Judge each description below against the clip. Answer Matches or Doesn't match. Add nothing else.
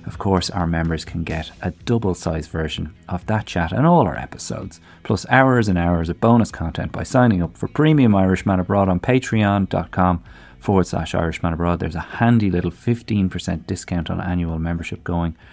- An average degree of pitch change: Matches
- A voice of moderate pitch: Doesn't match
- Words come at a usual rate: Matches